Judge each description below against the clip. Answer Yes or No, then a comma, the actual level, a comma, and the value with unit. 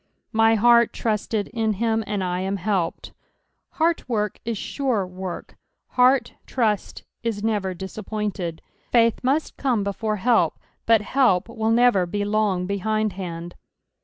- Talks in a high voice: Yes, high, 215 Hz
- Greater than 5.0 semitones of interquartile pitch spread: No, average, 3.2 semitones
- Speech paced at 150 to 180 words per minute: No, slow, 135 wpm